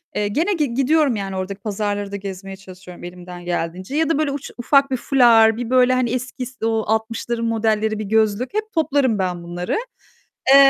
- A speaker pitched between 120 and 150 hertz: No, high, 220 Hz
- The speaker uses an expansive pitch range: No, average, 4.8 semitones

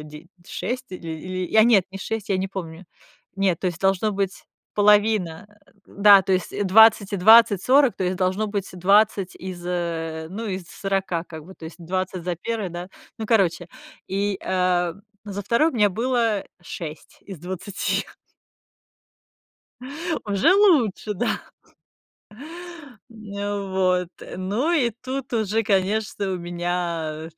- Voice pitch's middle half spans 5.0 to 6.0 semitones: No, average, 3.1 semitones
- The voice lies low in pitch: No, high, 190 Hz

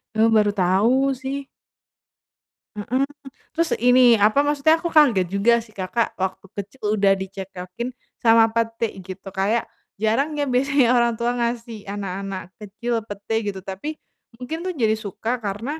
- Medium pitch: No, high, 225 Hz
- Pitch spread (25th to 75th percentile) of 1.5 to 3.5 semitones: No, average, 4.1 semitones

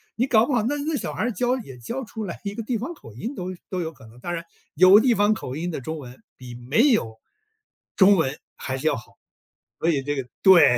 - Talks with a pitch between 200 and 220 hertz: No, medium, 185 Hz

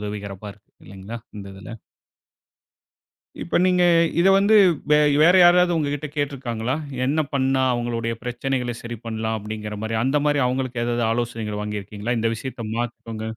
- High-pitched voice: No, low, 120 Hz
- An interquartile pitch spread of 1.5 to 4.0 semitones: Yes, average, 3.7 semitones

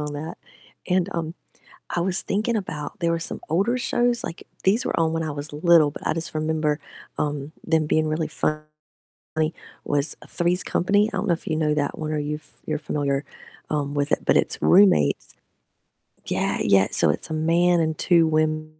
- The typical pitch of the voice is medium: Yes, medium, 155 Hz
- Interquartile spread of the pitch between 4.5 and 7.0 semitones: No, narrow, 2.4 semitones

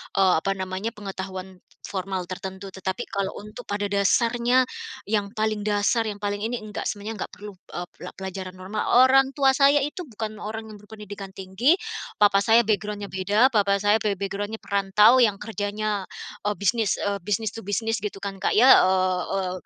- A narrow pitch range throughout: Yes, narrow, 2.2 semitones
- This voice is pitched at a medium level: No, high, 205 Hz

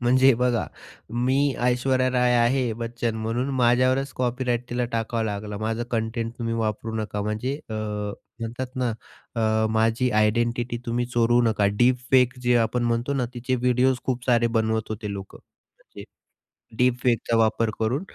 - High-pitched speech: No, low, 120 Hz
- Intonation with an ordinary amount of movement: No, narrow, 1.9 semitones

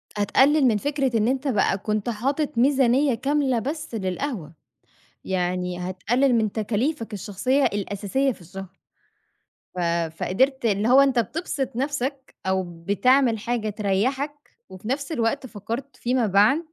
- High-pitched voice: Yes, high, 235 Hz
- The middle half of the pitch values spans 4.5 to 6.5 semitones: Yes, average, 5.2 semitones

